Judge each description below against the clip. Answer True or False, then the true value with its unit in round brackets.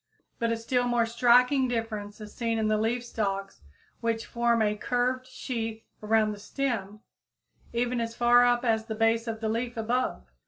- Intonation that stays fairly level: True (1.8 semitones)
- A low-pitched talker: False (230 Hz)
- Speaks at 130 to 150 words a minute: False (180 wpm)